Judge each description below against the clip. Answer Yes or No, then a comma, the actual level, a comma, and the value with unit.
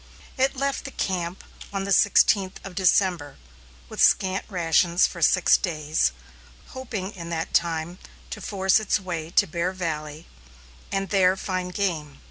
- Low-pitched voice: No, medium, 185 Hz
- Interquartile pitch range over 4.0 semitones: No, average, 2.7 semitones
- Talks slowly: No, average, 145 wpm